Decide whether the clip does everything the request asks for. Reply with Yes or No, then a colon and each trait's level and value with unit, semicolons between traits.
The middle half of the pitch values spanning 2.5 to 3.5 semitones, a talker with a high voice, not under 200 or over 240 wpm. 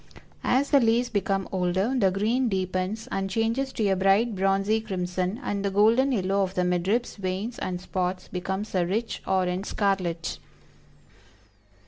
No: average, 3.2 semitones; high, 195 Hz; average, 155 wpm